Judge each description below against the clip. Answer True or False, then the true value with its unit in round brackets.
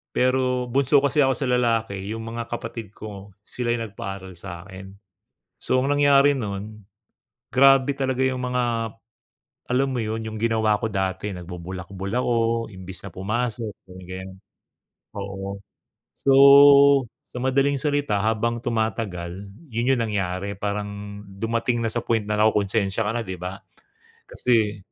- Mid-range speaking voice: False (110 Hz)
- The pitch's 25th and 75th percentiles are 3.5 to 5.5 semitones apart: True (4.0 semitones)